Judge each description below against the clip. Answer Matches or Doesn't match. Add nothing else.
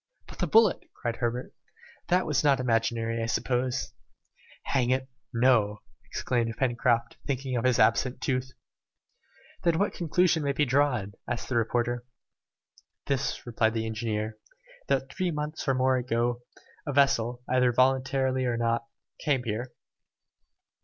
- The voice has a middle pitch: Doesn't match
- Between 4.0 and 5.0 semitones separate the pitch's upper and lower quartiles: Doesn't match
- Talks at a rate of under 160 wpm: Matches